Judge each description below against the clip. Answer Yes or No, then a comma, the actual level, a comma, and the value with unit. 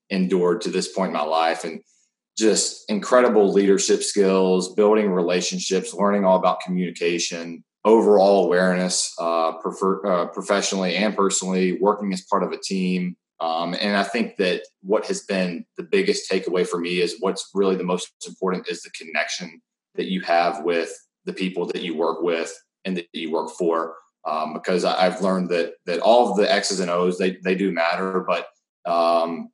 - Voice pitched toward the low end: Yes, very low, 90 Hz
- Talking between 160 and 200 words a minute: Yes, average, 175 wpm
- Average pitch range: No, narrow, 2.0 semitones